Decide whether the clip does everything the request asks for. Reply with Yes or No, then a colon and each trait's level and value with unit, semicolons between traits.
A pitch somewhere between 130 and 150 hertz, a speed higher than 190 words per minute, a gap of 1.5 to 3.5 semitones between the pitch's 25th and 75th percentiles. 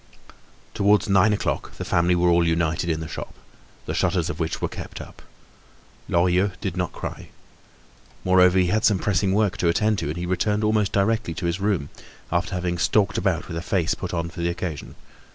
No: very low, 90 Hz; average, 200 wpm; narrow, 2.6 semitones